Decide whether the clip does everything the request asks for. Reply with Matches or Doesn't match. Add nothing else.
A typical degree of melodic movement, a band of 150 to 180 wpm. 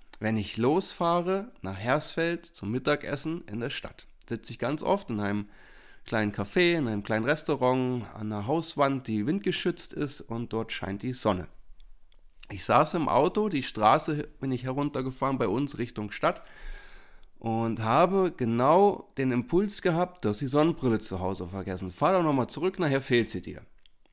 Doesn't match